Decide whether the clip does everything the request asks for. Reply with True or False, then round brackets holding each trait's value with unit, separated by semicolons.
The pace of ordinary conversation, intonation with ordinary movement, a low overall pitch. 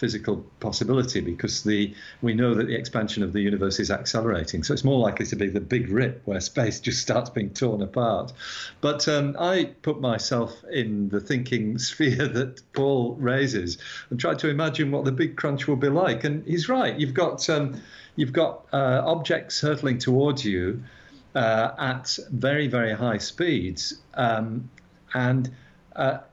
True (170 wpm; 4.1 semitones; 125 Hz)